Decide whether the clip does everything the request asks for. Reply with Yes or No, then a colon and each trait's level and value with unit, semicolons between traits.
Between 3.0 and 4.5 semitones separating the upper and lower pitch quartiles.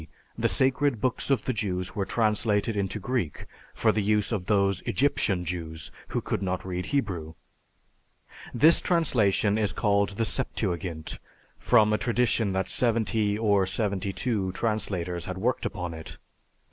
Yes: average, 3.5 semitones